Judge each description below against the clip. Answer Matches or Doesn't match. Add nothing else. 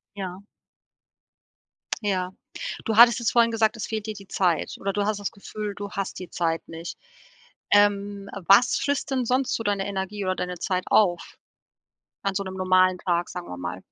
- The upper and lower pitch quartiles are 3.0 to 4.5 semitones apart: Doesn't match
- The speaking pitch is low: Doesn't match